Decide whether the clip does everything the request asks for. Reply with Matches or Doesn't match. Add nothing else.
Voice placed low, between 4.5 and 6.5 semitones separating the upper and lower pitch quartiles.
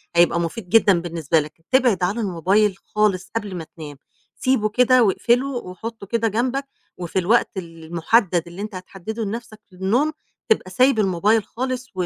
Doesn't match